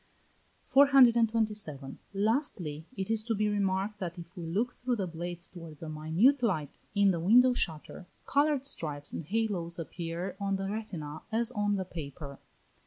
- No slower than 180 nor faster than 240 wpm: No, average, 160 wpm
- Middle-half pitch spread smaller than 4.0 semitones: No, average, 5.2 semitones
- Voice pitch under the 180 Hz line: No, high, 195 Hz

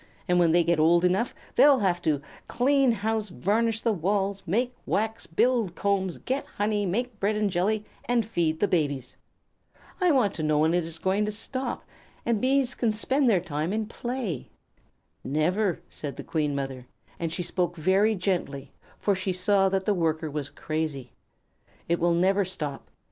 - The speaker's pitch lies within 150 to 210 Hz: Yes, high, 190 Hz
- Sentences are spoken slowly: No, average, 175 wpm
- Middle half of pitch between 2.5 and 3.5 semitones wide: No, average, 5.0 semitones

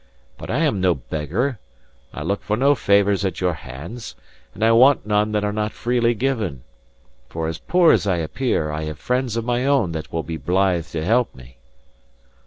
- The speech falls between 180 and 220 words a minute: Yes, average, 195 wpm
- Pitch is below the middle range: Yes, low, 105 Hz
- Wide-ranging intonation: Yes, wide, 6.8 semitones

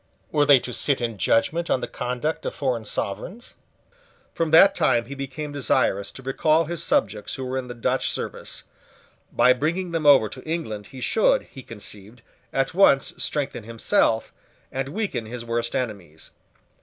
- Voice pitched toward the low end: Yes, low, 130 Hz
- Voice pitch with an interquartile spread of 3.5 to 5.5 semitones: Yes, average, 4.9 semitones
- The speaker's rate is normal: Yes, average, 170 wpm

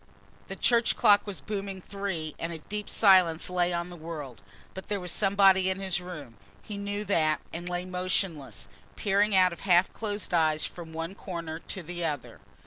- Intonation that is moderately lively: Yes, average, 3.0 semitones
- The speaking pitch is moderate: Yes, medium, 180 Hz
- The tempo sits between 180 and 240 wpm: Yes, average, 185 wpm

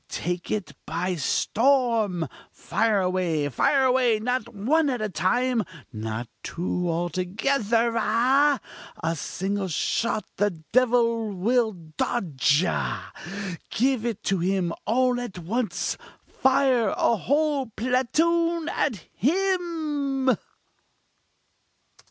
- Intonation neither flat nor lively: No, wide, 6.0 semitones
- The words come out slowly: Yes, slow, 105 wpm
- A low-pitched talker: No, high, 230 Hz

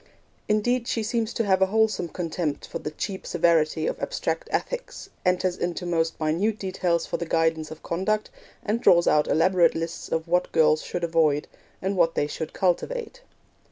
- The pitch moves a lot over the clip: No, average, 4.3 semitones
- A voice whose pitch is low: No, medium, 175 Hz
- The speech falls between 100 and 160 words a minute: No, average, 180 wpm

